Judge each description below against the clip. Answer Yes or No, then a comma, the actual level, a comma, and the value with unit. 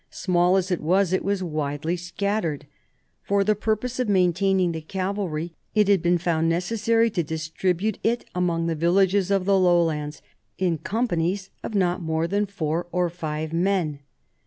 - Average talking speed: Yes, average, 160 wpm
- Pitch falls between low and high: Yes, medium, 180 Hz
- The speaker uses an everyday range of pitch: Yes, average, 3.2 semitones